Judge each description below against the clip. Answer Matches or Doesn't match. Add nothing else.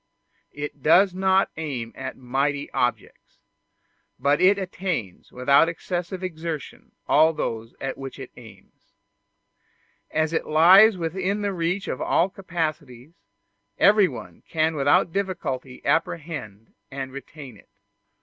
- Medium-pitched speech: Matches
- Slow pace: Matches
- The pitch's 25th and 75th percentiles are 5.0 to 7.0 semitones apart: Matches